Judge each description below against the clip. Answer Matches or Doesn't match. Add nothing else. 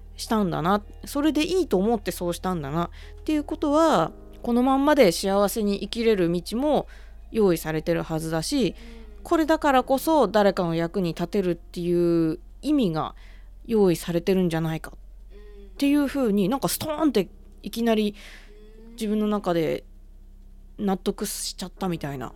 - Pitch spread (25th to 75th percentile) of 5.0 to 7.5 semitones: Matches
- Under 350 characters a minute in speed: Matches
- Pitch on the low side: Doesn't match